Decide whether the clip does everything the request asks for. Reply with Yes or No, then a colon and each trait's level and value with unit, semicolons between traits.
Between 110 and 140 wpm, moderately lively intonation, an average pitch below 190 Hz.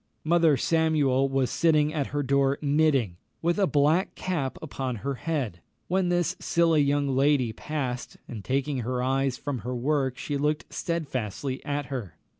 No: average, 160 wpm; average, 3.1 semitones; medium, 140 Hz